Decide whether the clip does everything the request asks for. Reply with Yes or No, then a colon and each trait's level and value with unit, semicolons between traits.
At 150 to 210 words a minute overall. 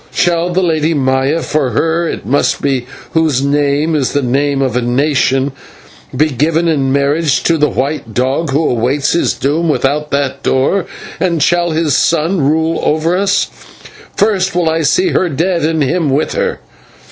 Yes: average, 170 wpm